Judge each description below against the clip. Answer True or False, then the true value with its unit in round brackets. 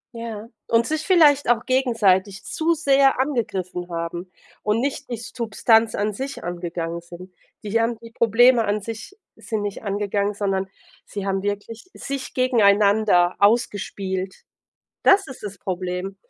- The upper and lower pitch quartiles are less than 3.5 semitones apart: False (3.9 semitones)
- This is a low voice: False (210 Hz)